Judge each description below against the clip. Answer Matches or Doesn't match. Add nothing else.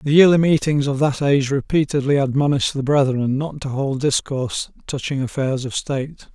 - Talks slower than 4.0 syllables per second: Doesn't match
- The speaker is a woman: Doesn't match